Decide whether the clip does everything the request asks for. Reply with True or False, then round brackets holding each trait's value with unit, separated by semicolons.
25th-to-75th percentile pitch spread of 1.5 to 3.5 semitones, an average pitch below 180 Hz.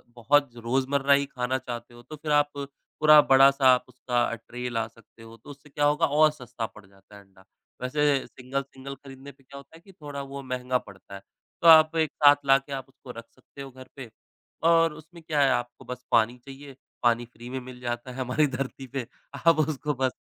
True (2.9 semitones; 135 Hz)